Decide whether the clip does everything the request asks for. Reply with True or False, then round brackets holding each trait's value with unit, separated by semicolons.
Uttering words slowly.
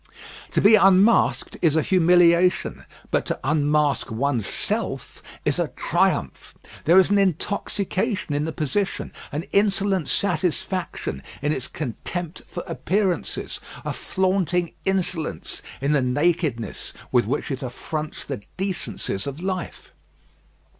True (125 wpm)